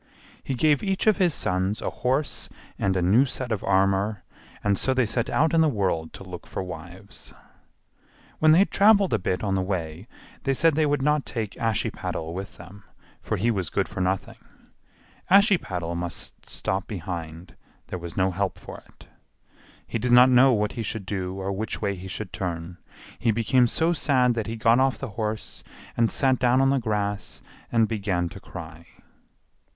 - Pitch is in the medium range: No, low, 105 Hz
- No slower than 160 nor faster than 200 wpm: Yes, average, 190 wpm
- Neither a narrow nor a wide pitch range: No, wide, 5.7 semitones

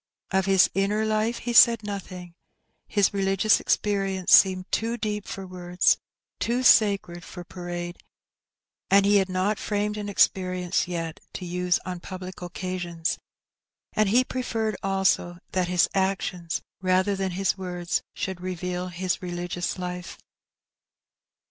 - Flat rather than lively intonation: Yes, narrow, 2.2 semitones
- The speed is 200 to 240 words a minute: No, slow, 135 wpm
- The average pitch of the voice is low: No, medium, 185 Hz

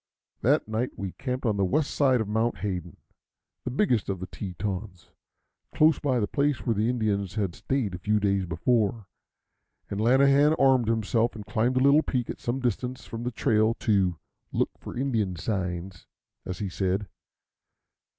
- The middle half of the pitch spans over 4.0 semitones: Yes, average, 4.4 semitones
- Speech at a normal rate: Yes, average, 170 wpm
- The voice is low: Yes, low, 110 Hz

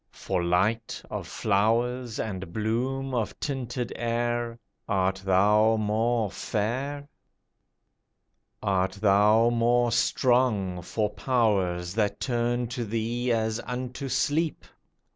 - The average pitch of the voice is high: No, low, 115 Hz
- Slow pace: Yes, slow, 105 wpm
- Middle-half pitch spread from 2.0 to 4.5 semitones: Yes, average, 2.9 semitones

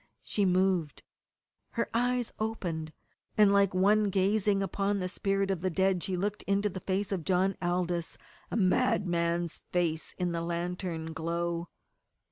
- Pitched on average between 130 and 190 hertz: Yes, medium, 185 Hz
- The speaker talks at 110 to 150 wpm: Yes, average, 145 wpm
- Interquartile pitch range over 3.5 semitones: No, narrow, 2.5 semitones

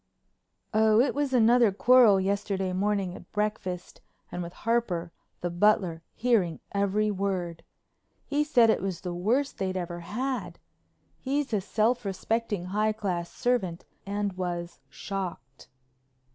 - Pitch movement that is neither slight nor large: Yes, average, 4.1 semitones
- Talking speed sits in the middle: No, slow, 130 wpm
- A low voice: No, high, 200 Hz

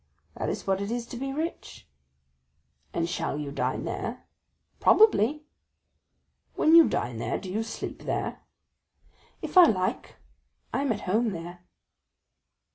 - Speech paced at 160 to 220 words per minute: No, average, 140 wpm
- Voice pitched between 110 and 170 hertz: No, high, 215 Hz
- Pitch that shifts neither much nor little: No, wide, 7.6 semitones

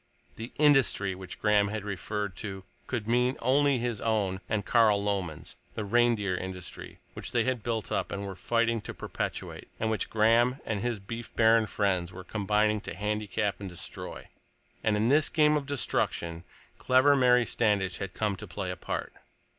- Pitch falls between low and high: No, low, 105 Hz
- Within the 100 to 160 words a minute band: No, average, 175 wpm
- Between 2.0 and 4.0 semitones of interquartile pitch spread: Yes, average, 3.3 semitones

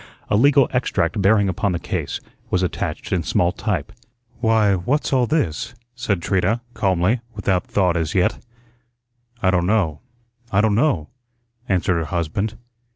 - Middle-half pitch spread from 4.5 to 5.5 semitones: No, average, 4.1 semitones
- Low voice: Yes, very low, 95 Hz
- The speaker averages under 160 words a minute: Yes, average, 150 wpm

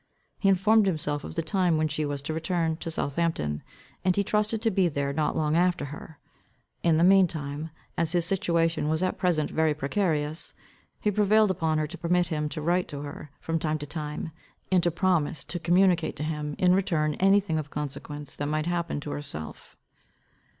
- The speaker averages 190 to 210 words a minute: Yes, average, 200 wpm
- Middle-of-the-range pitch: Yes, medium, 160 Hz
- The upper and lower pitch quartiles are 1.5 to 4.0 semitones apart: Yes, average, 3.2 semitones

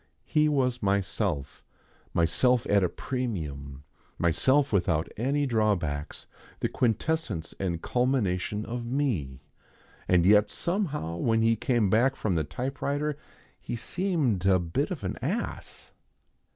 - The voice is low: Yes, low, 110 Hz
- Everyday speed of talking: No, slow, 125 wpm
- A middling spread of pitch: No, wide, 7.3 semitones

